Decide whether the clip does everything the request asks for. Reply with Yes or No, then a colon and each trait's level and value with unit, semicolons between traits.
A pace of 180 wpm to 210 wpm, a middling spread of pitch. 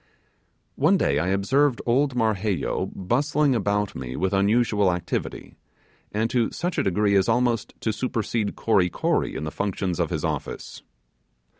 No: average, 150 wpm; average, 4.1 semitones